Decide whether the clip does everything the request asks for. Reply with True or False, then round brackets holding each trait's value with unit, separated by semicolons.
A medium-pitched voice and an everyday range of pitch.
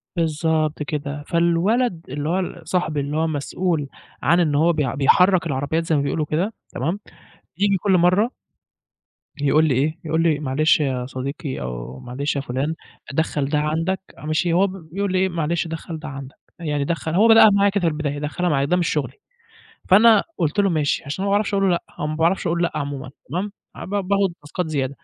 True (160 Hz; 3.7 semitones)